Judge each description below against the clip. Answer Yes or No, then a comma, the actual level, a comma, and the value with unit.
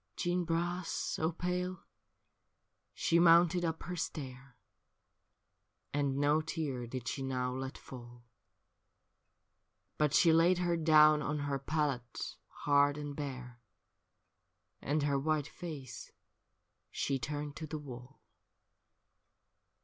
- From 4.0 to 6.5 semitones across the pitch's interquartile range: No, average, 3.5 semitones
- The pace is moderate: No, slow, 110 wpm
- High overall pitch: No, medium, 150 Hz